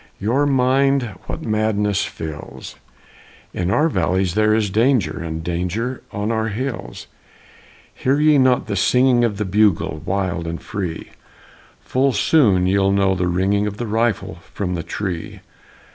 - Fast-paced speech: No, average, 145 wpm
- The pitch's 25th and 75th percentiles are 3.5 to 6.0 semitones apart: Yes, average, 4.8 semitones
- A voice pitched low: Yes, low, 105 Hz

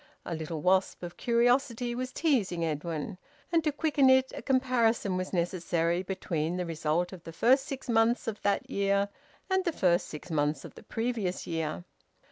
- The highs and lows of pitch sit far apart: Yes, wide, 6.6 semitones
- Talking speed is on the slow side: No, average, 175 wpm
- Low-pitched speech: No, high, 195 Hz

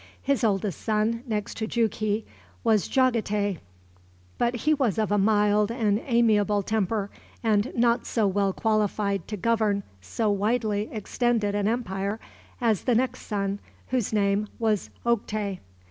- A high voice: Yes, high, 215 Hz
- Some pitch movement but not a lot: No, narrow, 2.2 semitones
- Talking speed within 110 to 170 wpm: Yes, average, 140 wpm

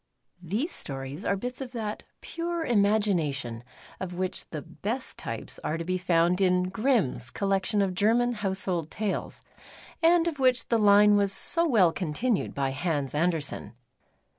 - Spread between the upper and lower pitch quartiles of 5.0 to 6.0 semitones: Yes, wide, 5.6 semitones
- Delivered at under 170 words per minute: Yes, average, 160 wpm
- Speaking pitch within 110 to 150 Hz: No, high, 195 Hz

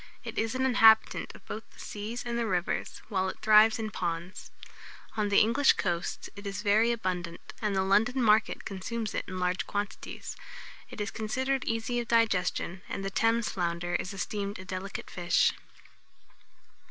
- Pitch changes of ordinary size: Yes, average, 3.3 semitones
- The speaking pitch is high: Yes, high, 210 Hz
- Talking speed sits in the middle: Yes, average, 170 wpm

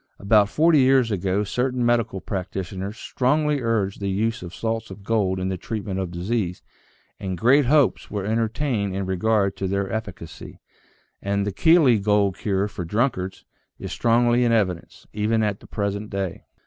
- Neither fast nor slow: Yes, average, 165 wpm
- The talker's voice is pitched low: Yes, low, 105 Hz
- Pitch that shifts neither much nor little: Yes, average, 3.4 semitones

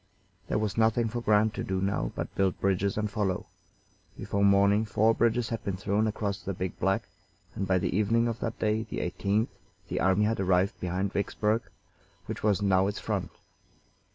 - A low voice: Yes, low, 100 Hz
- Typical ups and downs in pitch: No, narrow, 2.2 semitones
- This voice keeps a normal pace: Yes, average, 185 wpm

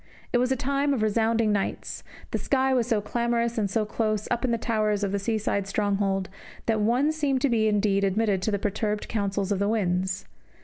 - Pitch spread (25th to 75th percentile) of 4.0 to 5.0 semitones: No, average, 2.7 semitones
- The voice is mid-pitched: No, high, 215 Hz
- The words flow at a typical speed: No, fast, 210 wpm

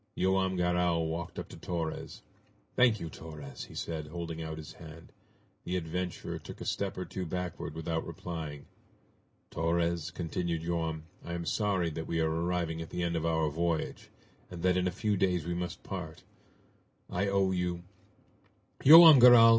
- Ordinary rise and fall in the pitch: No, narrow, 1.9 semitones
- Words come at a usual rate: Yes, average, 170 wpm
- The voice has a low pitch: Yes, very low, 85 Hz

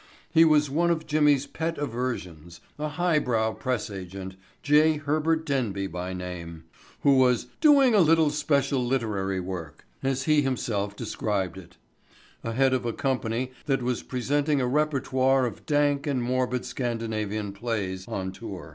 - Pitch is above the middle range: No, low, 125 Hz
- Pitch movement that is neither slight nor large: No, wide, 6.6 semitones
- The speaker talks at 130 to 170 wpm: Yes, average, 140 wpm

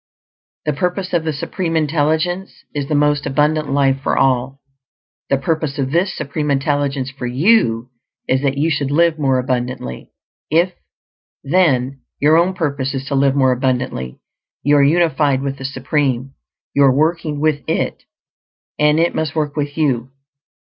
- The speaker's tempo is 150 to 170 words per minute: Yes, average, 160 wpm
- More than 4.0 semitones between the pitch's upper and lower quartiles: No, average, 2.8 semitones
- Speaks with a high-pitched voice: No, medium, 145 Hz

